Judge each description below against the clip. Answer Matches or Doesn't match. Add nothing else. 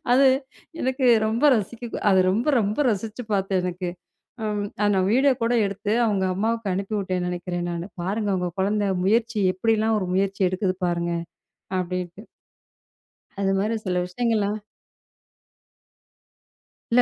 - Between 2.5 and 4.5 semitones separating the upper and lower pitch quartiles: Matches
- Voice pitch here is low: Doesn't match